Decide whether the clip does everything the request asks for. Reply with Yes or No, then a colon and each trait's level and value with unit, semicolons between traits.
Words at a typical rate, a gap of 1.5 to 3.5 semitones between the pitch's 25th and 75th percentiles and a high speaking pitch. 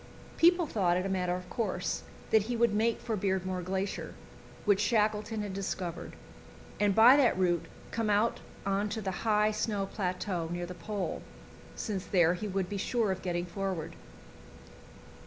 Yes: average, 165 wpm; average, 2.8 semitones; high, 195 Hz